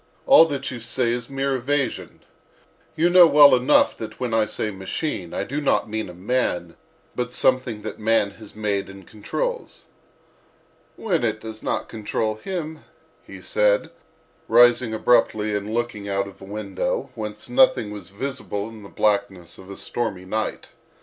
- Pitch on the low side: Yes, low, 110 Hz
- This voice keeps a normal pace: Yes, average, 165 wpm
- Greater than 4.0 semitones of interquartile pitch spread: Yes, average, 4.5 semitones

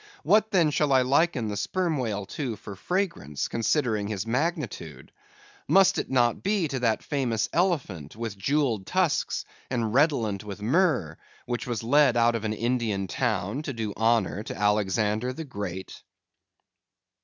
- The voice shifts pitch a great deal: Yes, wide, 5.9 semitones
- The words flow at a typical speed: Yes, average, 155 wpm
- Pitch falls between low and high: No, low, 120 Hz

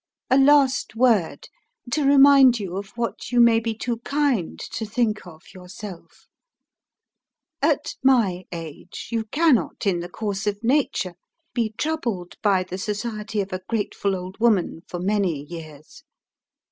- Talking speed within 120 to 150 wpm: Yes, average, 145 wpm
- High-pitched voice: Yes, high, 215 Hz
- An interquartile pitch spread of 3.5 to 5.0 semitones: Yes, average, 4.7 semitones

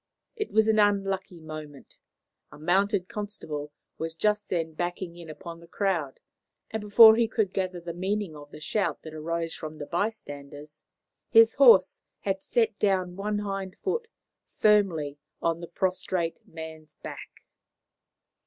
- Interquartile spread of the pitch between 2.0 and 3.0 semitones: No, average, 4.4 semitones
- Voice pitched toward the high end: No, medium, 180 Hz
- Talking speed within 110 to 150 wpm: Yes, average, 145 wpm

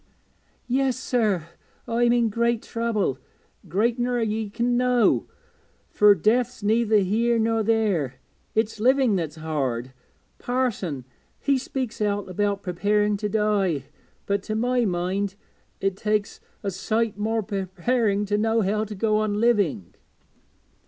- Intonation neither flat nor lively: Yes, average, 3.0 semitones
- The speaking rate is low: Yes, slow, 130 wpm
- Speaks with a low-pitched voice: No, high, 215 Hz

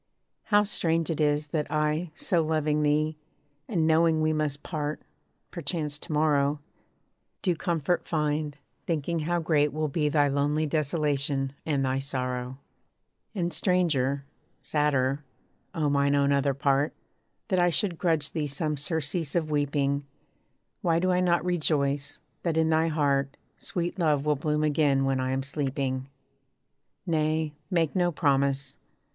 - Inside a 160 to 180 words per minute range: No, average, 145 wpm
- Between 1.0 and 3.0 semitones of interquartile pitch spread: Yes, narrow, 2.5 semitones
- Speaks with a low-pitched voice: No, medium, 150 Hz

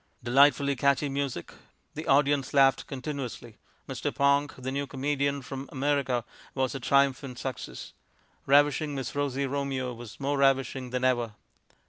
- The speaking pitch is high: No, low, 135 Hz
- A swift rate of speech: No, slow, 135 wpm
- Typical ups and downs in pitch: No, narrow, 1.5 semitones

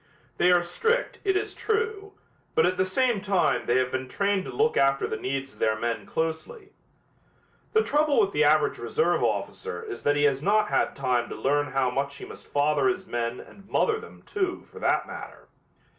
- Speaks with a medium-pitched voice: Yes, medium, 180 Hz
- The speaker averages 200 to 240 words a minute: Yes, fast, 205 wpm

